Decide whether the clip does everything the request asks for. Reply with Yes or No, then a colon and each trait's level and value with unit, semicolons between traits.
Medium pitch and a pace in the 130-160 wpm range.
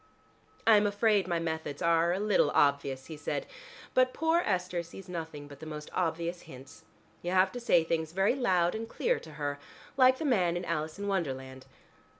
No: medium, 170 Hz; average, 190 wpm